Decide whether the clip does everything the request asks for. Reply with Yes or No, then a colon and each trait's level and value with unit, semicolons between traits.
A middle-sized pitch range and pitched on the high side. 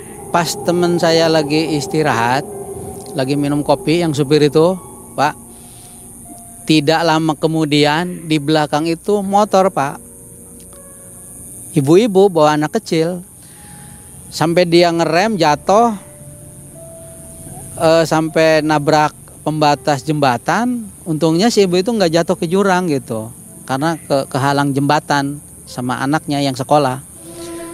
No: average, 3.0 semitones; medium, 155 Hz